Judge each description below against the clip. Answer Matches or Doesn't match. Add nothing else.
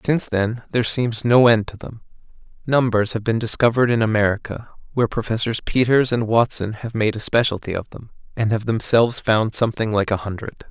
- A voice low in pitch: Matches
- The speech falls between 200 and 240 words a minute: Doesn't match